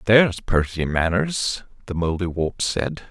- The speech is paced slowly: Yes, slow, 115 wpm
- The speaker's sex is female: No, male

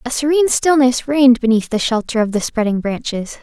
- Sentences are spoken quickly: No, average, 195 wpm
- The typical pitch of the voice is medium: No, high, 245 Hz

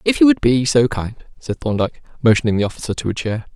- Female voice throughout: No, male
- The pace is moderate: No, fast, 235 wpm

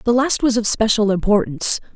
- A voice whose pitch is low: No, high, 220 Hz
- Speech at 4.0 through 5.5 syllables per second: No, 5.9 syllables/s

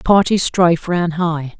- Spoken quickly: No, average, 150 wpm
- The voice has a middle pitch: Yes, medium, 170 Hz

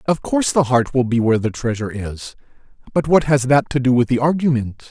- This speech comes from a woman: No, male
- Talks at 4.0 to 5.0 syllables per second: No, 6.0 syllables/s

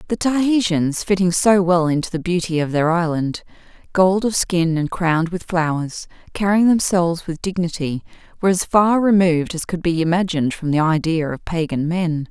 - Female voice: Yes, female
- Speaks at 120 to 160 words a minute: No, average, 175 wpm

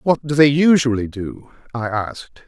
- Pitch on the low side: Yes, low, 130 Hz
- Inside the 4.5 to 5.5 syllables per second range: Yes, 5.0 syllables/s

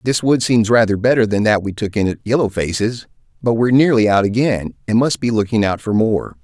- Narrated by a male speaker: Yes, male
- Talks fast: Yes, fast, 235 wpm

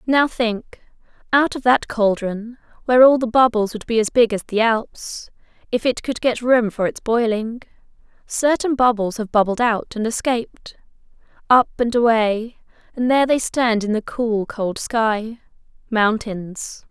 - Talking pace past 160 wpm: No, average, 155 wpm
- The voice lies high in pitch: Yes, high, 230 Hz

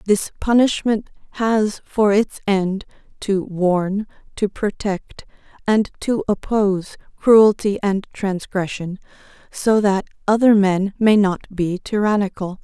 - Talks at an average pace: No, slow, 115 wpm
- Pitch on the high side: Yes, high, 200 Hz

